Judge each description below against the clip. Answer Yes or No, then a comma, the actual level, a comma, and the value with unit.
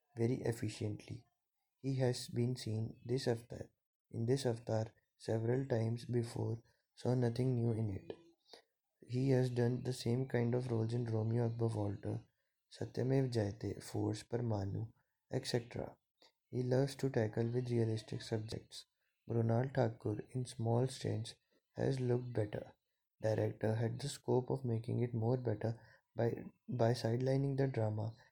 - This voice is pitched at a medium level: No, low, 120 Hz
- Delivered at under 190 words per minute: Yes, average, 140 wpm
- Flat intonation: Yes, narrow, 2.1 semitones